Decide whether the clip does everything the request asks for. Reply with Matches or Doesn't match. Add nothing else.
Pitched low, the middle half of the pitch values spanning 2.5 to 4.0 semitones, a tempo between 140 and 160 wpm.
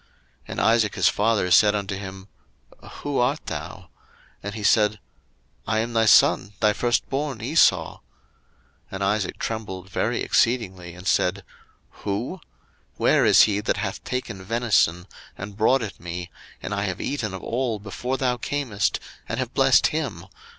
Matches